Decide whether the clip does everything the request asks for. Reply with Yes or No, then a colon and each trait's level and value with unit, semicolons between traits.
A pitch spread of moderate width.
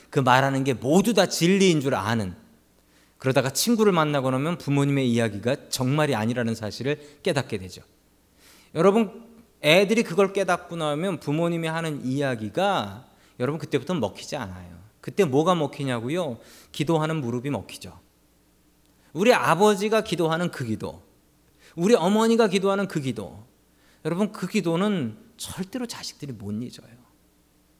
No: wide, 7.5 semitones